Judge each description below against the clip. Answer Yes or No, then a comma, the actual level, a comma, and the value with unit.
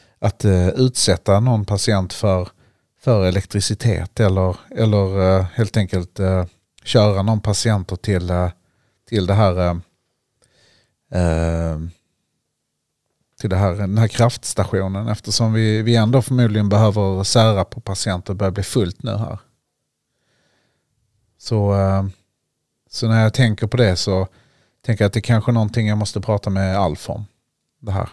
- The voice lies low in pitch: Yes, low, 105 Hz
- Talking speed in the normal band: Yes, average, 145 wpm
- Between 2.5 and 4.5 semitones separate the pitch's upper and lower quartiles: Yes, average, 2.9 semitones